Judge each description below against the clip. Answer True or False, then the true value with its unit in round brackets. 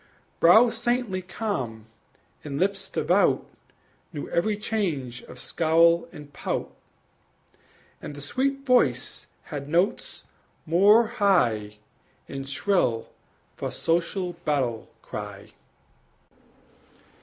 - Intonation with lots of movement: True (6.7 semitones)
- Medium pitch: True (170 Hz)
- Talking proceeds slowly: True (95 wpm)